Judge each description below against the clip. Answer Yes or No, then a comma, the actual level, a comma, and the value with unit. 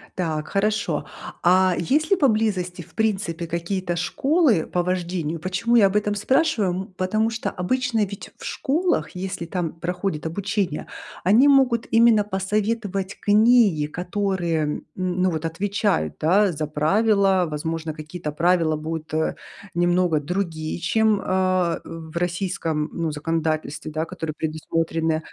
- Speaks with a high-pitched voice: No, medium, 180 Hz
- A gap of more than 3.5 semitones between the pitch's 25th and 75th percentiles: Yes, average, 4.1 semitones